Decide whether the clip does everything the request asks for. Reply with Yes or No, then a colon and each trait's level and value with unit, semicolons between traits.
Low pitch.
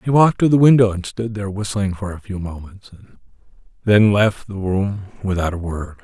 Yes: low, 100 Hz